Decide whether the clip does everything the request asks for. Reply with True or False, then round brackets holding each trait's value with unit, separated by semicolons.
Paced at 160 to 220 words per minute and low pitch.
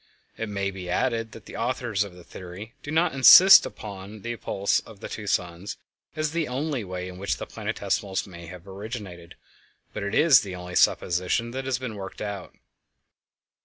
True (180 wpm; 100 Hz)